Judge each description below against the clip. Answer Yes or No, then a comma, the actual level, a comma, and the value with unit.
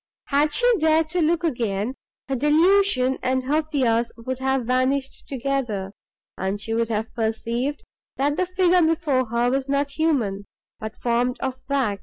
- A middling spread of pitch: Yes, average, 4.4 semitones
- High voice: Yes, very high, 265 Hz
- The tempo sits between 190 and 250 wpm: No, average, 160 wpm